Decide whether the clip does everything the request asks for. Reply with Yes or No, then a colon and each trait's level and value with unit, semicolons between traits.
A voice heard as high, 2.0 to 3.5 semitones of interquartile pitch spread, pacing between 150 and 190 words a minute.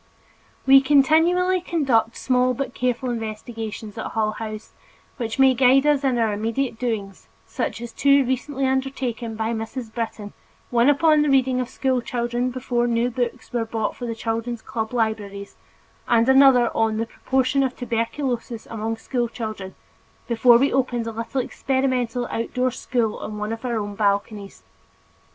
Yes: high, 240 Hz; average, 2.7 semitones; average, 155 wpm